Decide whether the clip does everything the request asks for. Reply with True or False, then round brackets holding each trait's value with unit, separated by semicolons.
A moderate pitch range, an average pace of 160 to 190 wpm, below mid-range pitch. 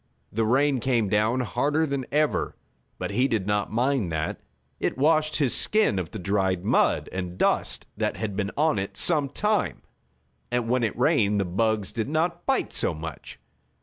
False (6.3 semitones; 180 wpm; 120 Hz)